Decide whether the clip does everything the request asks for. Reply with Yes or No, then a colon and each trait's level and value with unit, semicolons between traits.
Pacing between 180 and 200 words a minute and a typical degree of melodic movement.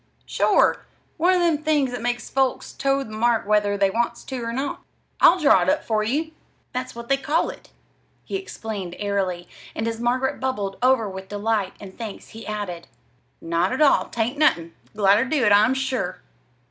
Yes: average, 190 wpm; average, 4.6 semitones